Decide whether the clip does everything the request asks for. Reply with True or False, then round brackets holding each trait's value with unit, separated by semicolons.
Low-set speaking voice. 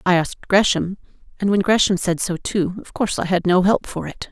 False (190 Hz)